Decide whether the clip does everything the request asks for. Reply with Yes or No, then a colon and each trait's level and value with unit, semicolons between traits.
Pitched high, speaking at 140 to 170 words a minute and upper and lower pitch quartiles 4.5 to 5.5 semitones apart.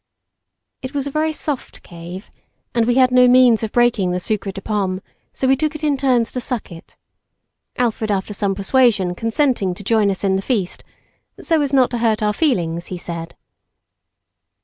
No: high, 225 Hz; average, 190 wpm; average, 5.1 semitones